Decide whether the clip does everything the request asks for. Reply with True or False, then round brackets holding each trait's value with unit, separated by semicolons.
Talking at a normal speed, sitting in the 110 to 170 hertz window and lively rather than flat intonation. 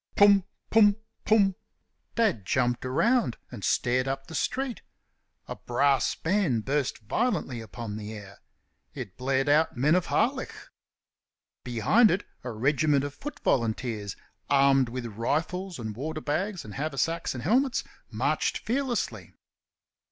False (130 wpm; 140 Hz; 8.0 semitones)